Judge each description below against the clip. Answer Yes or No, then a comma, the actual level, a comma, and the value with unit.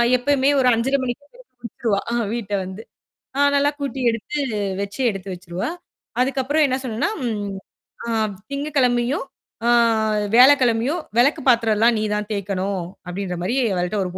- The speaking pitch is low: No, high, 235 Hz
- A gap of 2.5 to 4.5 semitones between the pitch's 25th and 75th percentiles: No, average, 4.9 semitones